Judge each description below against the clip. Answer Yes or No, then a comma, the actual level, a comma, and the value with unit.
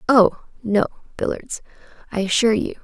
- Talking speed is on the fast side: No, slow, 125 wpm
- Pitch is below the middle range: No, high, 220 Hz